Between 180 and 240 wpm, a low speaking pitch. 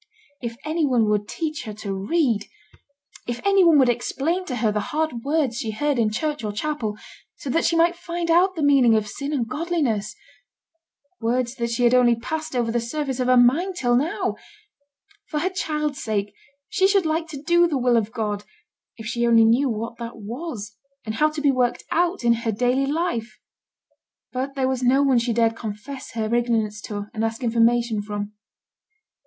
No: average, 195 wpm; high, 245 Hz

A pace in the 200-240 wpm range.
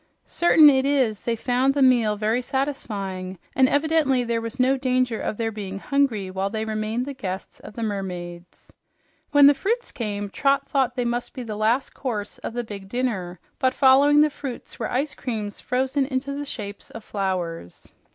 No: average, 185 wpm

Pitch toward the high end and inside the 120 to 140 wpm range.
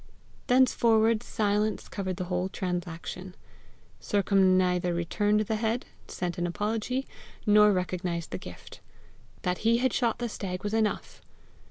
Yes: high, 200 Hz; slow, 135 wpm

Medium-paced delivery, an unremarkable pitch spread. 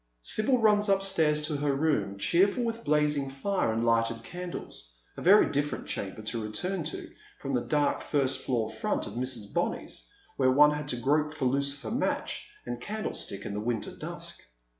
No: average, 180 wpm; wide, 6.1 semitones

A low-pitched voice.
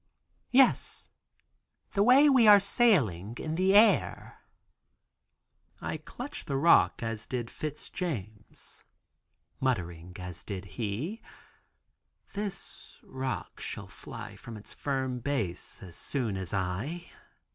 Yes: low, 130 Hz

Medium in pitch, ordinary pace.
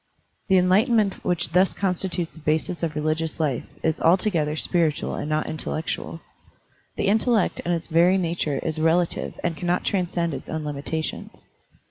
Yes: medium, 170 Hz; average, 160 wpm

